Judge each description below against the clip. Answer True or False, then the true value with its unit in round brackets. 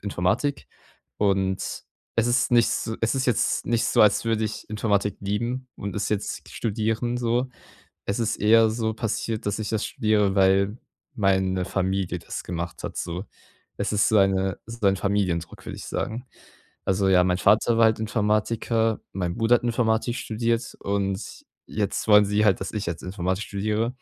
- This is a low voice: True (105 Hz)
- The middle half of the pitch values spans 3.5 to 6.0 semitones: False (2.8 semitones)